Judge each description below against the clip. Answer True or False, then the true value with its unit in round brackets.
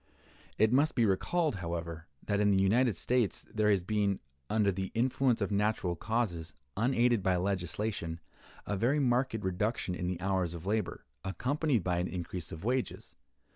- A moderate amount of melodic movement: True (4.6 semitones)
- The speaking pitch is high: False (100 Hz)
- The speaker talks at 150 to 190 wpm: True (165 wpm)